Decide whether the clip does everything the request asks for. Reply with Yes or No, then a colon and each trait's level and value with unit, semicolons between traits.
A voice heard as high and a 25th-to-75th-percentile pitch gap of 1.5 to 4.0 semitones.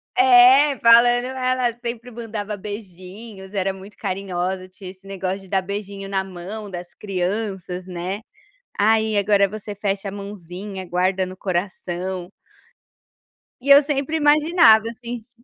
Yes: high, 200 Hz; average, 3.7 semitones